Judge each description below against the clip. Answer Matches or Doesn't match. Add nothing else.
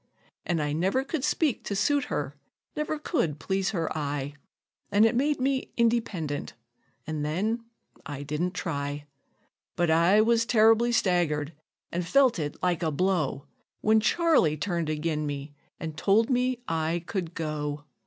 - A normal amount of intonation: Doesn't match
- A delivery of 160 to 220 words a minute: Doesn't match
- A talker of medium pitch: Matches